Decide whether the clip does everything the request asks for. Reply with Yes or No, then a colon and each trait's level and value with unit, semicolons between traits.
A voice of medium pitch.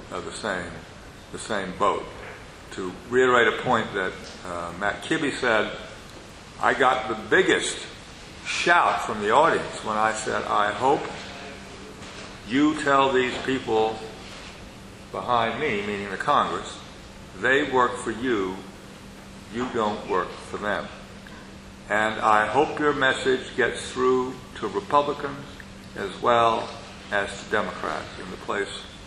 No: low, 115 Hz